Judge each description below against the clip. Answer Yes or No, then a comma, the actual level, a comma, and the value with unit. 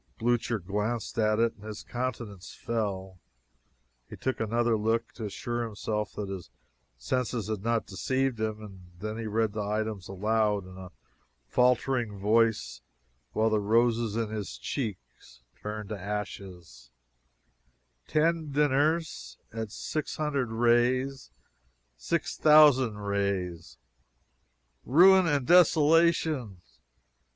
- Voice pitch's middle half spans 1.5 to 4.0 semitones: Yes, average, 3.7 semitones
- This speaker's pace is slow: Yes, slow, 110 wpm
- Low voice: Yes, low, 110 Hz